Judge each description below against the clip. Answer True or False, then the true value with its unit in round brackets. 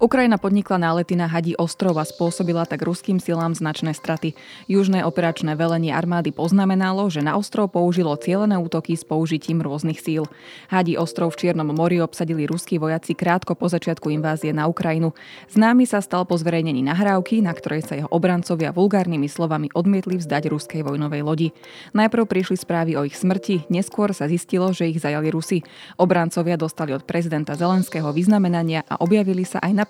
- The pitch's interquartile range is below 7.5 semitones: True (2.7 semitones)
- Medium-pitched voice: True (170 Hz)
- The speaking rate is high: True (170 wpm)